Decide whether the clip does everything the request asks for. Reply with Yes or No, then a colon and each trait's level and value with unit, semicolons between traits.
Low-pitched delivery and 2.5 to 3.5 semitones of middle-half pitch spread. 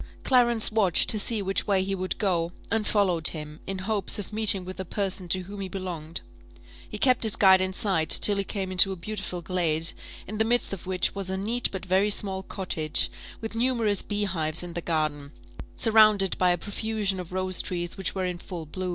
No: high, 190 Hz; average, 2.8 semitones